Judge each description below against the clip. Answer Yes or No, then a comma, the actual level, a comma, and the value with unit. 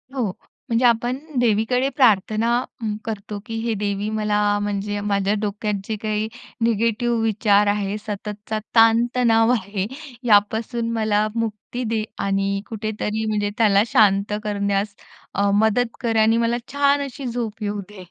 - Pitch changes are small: Yes, narrow, 2.0 semitones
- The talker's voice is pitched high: Yes, high, 215 Hz